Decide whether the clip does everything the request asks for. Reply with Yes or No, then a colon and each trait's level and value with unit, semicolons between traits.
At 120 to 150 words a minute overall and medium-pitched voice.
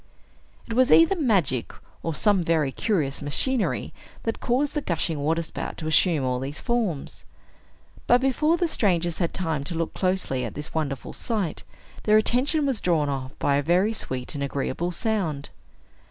No: average, 165 wpm; medium, 170 Hz